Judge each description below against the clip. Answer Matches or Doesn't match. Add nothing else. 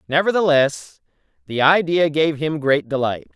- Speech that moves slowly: Matches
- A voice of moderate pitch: Matches